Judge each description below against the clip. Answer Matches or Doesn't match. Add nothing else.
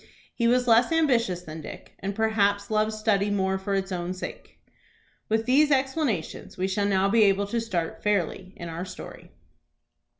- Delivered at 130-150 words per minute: Doesn't match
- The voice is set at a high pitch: Matches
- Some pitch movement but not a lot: Matches